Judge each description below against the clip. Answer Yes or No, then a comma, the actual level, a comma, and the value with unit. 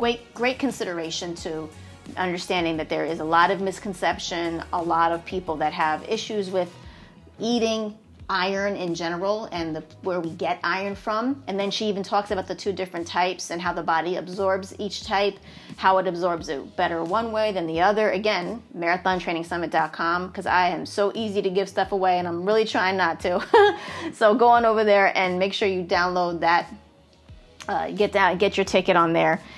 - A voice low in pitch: No, medium, 185 Hz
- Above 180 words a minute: Yes, average, 190 wpm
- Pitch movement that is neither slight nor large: Yes, average, 3.1 semitones